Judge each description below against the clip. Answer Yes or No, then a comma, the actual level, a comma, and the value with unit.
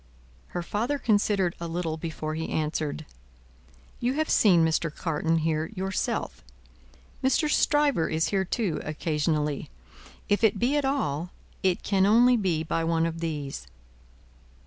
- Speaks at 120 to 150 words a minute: Yes, average, 140 wpm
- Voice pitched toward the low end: No, medium, 170 Hz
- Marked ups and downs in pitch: No, average, 4.9 semitones